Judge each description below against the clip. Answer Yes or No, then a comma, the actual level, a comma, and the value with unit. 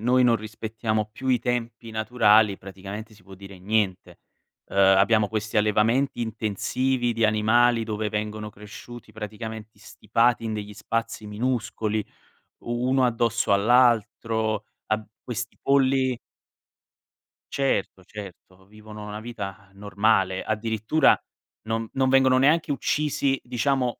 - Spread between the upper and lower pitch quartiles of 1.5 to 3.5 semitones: Yes, narrow, 2.5 semitones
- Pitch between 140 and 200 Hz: No, low, 110 Hz